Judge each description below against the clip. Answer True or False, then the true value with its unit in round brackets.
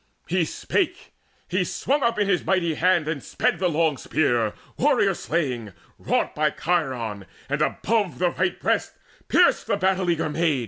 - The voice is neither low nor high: True (165 Hz)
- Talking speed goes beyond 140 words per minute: True (165 wpm)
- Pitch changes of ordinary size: True (4.8 semitones)